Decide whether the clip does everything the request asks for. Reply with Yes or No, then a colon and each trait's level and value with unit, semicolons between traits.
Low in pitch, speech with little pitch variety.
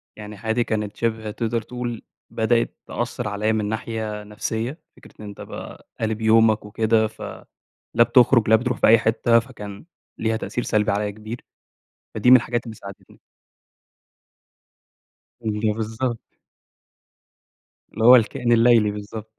Yes: low, 110 Hz; narrow, 1.8 semitones